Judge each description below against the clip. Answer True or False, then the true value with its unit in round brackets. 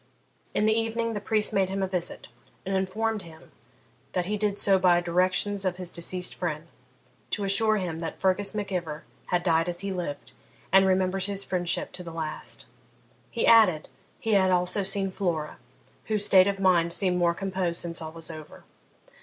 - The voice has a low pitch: False (185 Hz)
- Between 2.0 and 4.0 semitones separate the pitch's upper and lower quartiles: True (2.5 semitones)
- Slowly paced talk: False (185 wpm)